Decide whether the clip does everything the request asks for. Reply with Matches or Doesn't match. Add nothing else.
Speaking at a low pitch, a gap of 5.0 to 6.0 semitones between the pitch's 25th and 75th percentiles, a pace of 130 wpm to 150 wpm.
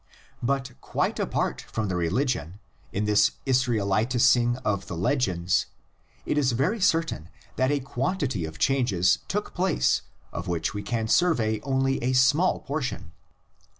Matches